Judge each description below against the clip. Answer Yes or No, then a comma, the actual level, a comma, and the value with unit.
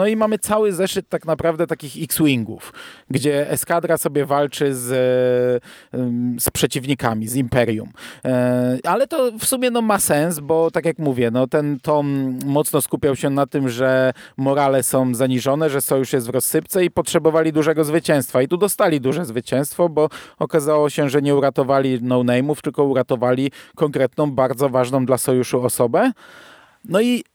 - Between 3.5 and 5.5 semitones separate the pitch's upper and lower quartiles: Yes, average, 3.9 semitones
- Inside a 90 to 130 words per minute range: No, fast, 160 wpm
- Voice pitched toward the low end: No, medium, 145 Hz